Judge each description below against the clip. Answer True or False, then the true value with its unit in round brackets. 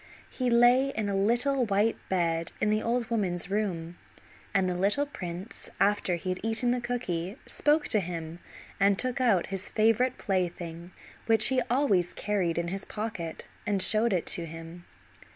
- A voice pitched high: True (200 Hz)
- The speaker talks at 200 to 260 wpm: False (170 wpm)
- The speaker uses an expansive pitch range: False (4.9 semitones)